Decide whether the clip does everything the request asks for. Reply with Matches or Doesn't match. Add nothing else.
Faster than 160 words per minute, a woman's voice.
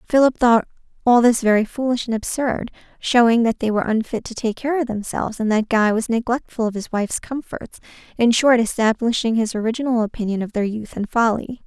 Matches